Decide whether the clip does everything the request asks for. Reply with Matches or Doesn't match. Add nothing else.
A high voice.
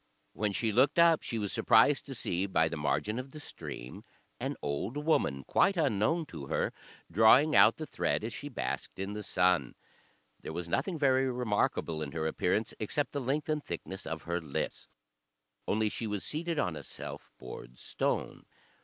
Doesn't match